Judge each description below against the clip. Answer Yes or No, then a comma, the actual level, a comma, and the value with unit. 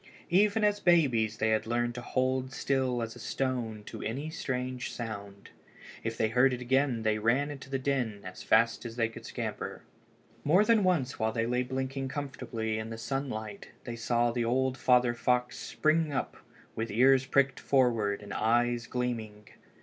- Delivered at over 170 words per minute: Yes, average, 185 wpm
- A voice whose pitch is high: No, low, 125 Hz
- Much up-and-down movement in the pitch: No, average, 2.9 semitones